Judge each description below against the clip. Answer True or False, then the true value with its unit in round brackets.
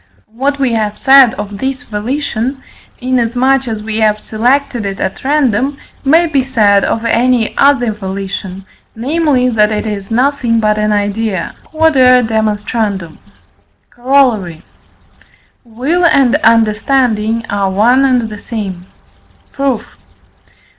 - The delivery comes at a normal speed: False (120 wpm)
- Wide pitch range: False (4.0 semitones)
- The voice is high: True (230 Hz)